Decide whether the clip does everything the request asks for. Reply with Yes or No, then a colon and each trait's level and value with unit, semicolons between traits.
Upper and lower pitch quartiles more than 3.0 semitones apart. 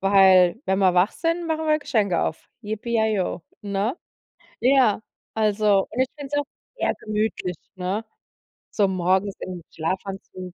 Yes: average, 3.7 semitones